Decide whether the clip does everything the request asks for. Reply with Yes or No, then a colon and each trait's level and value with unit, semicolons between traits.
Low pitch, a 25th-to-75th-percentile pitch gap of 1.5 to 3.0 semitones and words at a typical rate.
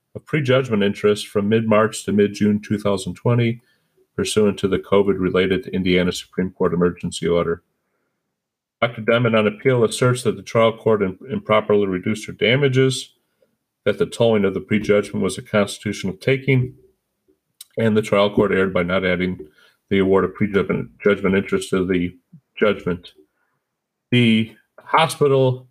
No: low, 105 Hz; average, 4.1 semitones; average, 145 wpm